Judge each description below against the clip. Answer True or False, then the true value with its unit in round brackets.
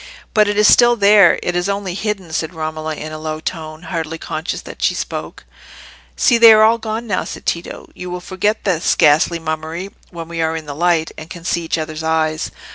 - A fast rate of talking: True (210 wpm)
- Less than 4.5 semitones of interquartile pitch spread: True (4.0 semitones)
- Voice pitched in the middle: True (170 Hz)